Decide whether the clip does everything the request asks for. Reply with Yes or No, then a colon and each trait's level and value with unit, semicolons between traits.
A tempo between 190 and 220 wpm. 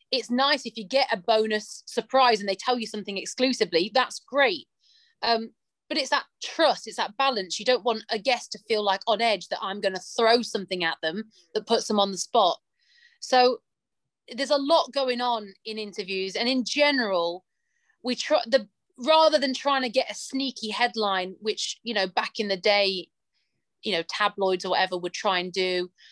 Yes: average, 200 wpm